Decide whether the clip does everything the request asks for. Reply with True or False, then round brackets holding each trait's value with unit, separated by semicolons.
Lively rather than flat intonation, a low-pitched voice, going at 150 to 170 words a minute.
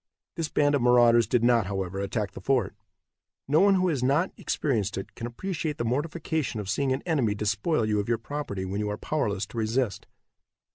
False (5.9 semitones; 120 Hz; 200 wpm)